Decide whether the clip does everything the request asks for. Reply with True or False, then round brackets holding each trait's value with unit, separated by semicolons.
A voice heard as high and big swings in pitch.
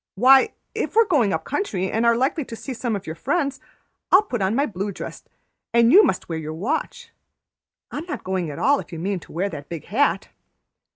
True (230 Hz; 7.4 semitones)